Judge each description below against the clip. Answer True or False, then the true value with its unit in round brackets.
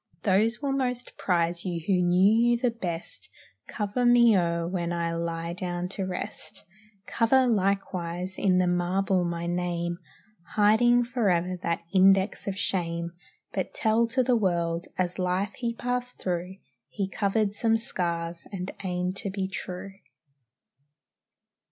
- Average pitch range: True (4.1 semitones)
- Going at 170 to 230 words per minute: False (140 wpm)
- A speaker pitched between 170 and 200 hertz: True (190 Hz)